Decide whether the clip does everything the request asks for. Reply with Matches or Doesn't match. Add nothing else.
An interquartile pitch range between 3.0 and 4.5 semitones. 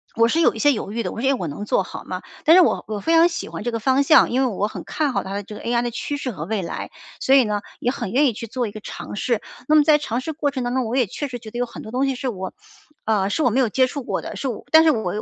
Matches